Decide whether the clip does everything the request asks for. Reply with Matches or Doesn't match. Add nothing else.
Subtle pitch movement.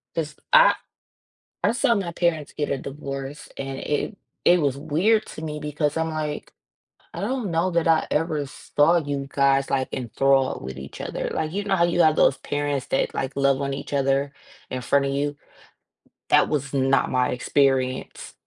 Doesn't match